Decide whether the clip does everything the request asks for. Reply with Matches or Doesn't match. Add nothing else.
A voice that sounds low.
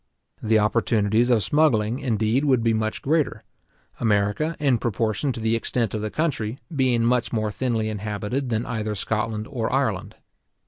Matches